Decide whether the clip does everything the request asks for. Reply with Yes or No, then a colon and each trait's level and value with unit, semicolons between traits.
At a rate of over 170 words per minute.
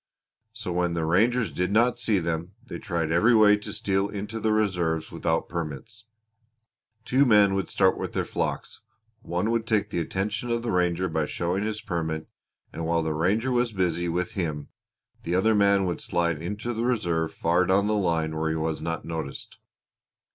Yes: average, 185 wpm